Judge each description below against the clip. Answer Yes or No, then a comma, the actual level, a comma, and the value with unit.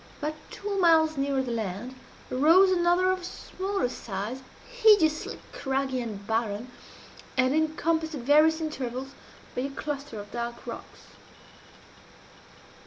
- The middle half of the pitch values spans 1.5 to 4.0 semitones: No, average, 4.9 semitones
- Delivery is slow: Yes, slow, 120 wpm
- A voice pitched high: Yes, very high, 280 Hz